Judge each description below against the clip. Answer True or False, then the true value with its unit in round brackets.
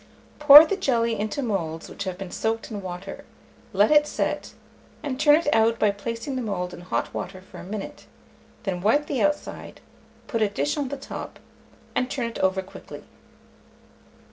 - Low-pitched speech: False (225 Hz)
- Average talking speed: True (180 wpm)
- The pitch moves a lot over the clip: True (6.1 semitones)